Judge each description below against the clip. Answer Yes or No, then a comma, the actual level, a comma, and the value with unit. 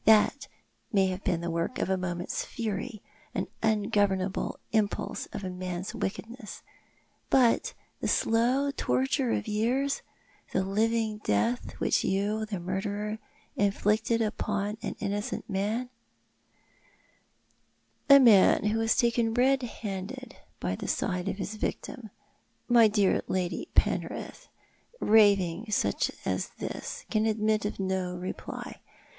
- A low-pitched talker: No, high, 210 Hz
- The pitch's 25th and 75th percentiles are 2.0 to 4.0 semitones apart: Yes, average, 3.0 semitones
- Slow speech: Yes, slow, 130 wpm